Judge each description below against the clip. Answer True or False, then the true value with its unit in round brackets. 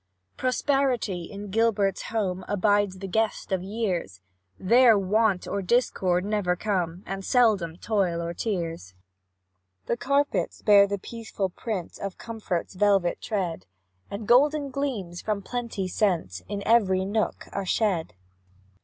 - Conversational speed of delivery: False (130 wpm)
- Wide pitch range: False (3.6 semitones)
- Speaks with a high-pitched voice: True (200 Hz)